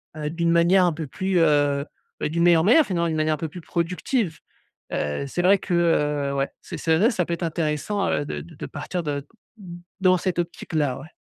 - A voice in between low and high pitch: Yes, medium, 170 Hz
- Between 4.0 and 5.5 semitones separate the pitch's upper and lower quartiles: No, average, 2.9 semitones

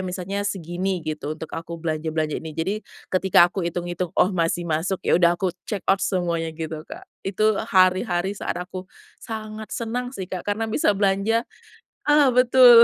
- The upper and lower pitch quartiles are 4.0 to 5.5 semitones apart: No, average, 3.3 semitones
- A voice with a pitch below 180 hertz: No, medium, 185 Hz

